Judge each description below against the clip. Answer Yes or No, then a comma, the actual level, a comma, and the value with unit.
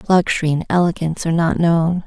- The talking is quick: No, average, 175 wpm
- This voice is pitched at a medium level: Yes, medium, 170 Hz